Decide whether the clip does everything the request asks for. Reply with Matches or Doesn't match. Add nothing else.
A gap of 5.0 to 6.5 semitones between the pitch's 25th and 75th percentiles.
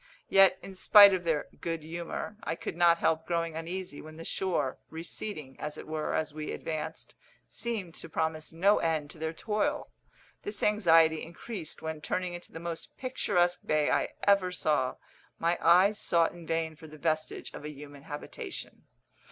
Doesn't match